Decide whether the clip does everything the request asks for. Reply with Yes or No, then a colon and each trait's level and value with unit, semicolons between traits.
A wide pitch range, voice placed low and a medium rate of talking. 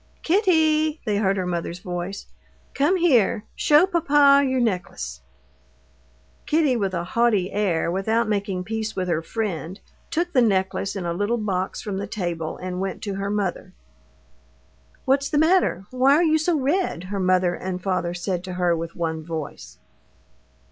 No: wide, 7.0 semitones; high, 200 Hz; average, 160 wpm